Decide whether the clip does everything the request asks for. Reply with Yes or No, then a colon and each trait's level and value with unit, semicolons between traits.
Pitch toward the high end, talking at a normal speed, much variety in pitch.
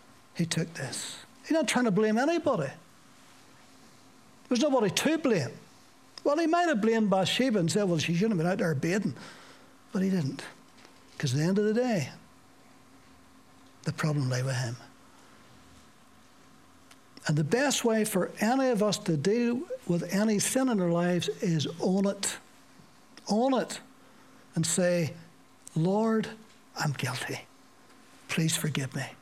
Yes: high, 200 Hz; average, 150 wpm; wide, 6.6 semitones